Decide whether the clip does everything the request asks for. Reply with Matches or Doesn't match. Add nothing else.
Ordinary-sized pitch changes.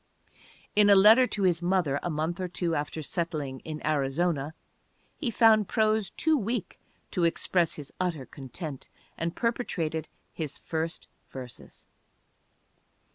Matches